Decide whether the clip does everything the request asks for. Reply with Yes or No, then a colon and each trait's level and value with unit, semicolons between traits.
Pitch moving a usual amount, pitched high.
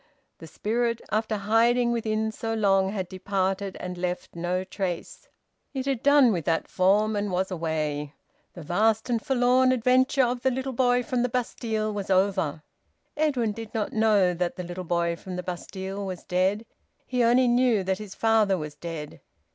Yes: average, 4.6 semitones; high, 205 Hz